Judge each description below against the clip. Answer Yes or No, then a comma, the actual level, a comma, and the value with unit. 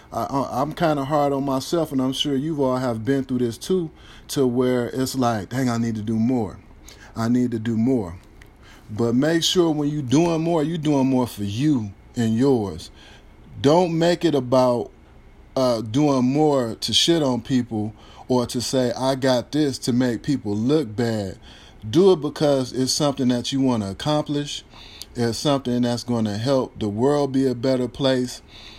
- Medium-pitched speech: No, low, 130 Hz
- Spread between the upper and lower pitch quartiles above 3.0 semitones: Yes, average, 3.7 semitones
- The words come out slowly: No, average, 190 wpm